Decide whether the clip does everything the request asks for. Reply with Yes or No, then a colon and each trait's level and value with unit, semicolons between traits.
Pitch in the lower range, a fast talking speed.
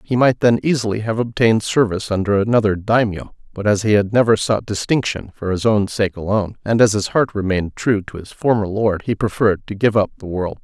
Yes: low, 105 Hz; fast, 220 wpm